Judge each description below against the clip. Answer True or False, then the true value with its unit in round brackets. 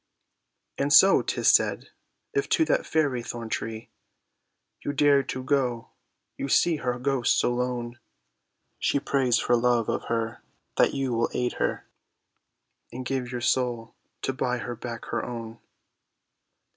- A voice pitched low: True (125 Hz)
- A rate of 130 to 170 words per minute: True (145 wpm)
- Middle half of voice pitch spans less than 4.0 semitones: True (2.4 semitones)